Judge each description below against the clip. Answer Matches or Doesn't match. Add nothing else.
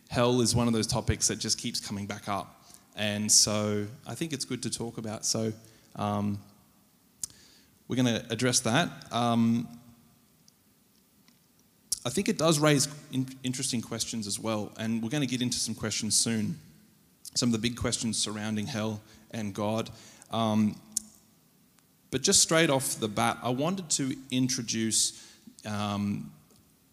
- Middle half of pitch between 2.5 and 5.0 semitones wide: Matches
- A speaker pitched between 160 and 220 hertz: Doesn't match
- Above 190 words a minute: Doesn't match